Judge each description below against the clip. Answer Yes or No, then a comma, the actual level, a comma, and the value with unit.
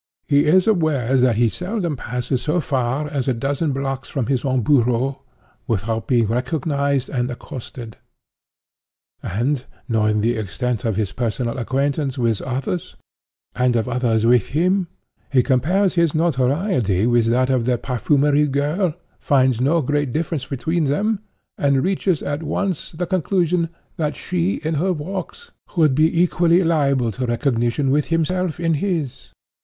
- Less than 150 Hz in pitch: Yes, medium, 140 Hz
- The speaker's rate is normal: Yes, average, 150 wpm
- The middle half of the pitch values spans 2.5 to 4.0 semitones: No, average, 4.9 semitones